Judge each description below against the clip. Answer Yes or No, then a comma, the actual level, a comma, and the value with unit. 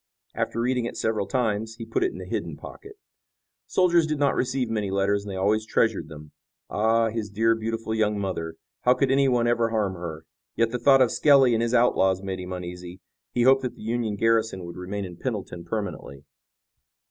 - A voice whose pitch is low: Yes, low, 110 Hz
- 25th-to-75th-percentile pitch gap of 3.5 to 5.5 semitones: Yes, average, 4.0 semitones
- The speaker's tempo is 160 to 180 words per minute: No, average, 200 wpm